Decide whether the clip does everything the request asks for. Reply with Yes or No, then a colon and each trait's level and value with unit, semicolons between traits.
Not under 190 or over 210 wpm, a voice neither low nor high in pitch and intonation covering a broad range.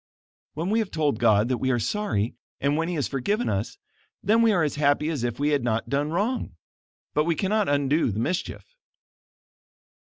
Yes: average, 195 wpm; medium, 150 Hz; wide, 7.1 semitones